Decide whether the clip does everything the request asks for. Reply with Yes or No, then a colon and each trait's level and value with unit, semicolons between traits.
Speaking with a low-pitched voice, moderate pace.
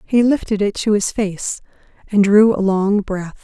No: high, 205 Hz; average, 190 wpm